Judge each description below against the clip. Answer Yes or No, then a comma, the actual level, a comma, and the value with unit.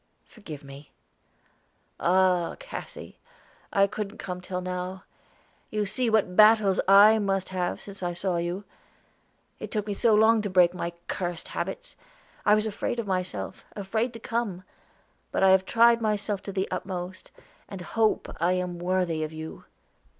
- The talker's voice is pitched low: No, high, 190 Hz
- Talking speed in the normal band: Yes, average, 160 wpm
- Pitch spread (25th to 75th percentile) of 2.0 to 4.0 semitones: Yes, average, 2.9 semitones